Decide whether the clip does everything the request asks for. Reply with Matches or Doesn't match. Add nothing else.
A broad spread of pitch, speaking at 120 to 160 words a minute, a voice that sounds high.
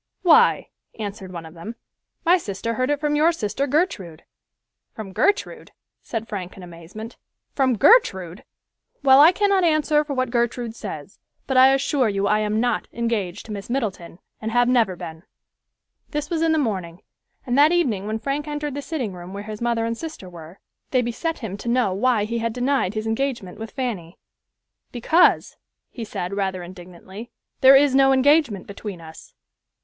Doesn't match